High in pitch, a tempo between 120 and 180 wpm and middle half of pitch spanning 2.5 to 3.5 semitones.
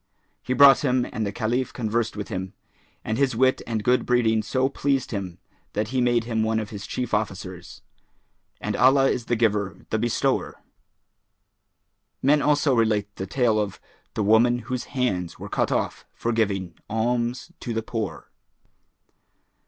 No: low, 115 Hz; average, 160 wpm; average, 3.0 semitones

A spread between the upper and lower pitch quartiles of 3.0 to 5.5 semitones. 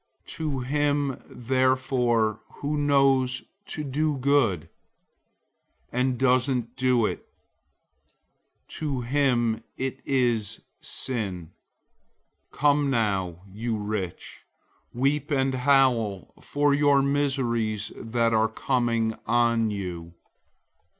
Yes: average, 3.6 semitones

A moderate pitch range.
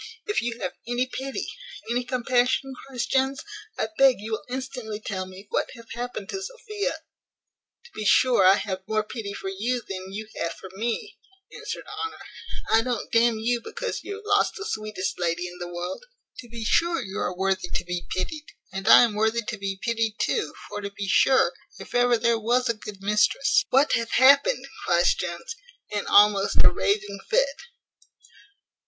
Yes: average, 4.5 semitones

